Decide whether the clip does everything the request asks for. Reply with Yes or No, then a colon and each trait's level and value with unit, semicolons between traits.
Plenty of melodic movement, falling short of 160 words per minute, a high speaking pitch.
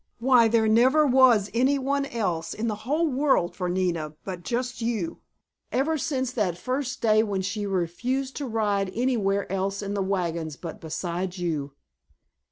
No: wide, 5.8 semitones; average, 165 wpm; high, 215 Hz